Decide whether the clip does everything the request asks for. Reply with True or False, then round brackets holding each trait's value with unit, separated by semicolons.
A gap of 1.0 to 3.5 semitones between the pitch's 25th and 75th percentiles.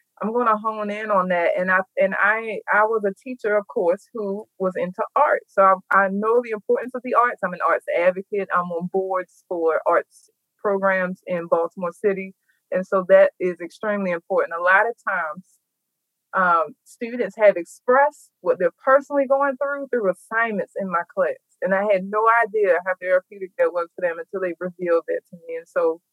False (4.8 semitones)